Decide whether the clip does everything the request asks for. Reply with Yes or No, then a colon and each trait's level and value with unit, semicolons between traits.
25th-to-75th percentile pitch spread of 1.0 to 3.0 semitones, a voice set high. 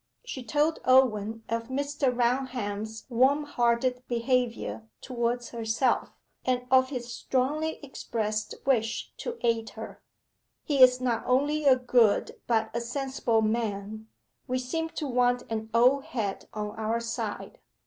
Yes: narrow, 2.6 semitones; high, 245 Hz